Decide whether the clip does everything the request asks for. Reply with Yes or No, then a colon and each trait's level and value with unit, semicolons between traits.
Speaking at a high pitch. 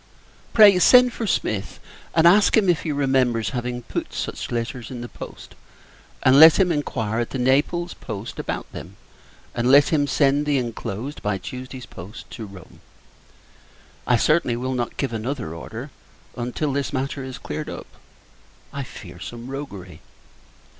No: low, 130 Hz